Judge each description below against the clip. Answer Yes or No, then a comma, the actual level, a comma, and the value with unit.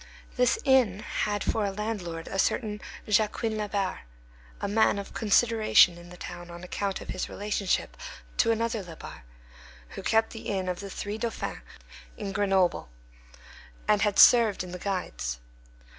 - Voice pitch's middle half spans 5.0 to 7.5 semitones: No, average, 3.1 semitones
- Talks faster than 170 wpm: No, average, 155 wpm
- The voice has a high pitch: Yes, high, 205 Hz